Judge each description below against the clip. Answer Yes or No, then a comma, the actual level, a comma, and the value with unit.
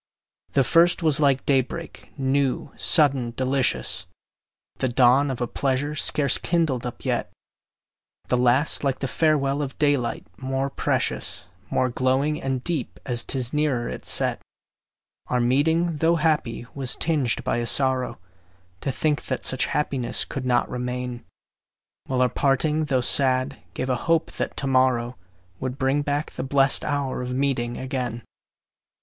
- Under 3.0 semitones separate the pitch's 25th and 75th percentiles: Yes, narrow, 2.4 semitones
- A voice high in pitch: No, low, 135 Hz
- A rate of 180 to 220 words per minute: No, average, 150 wpm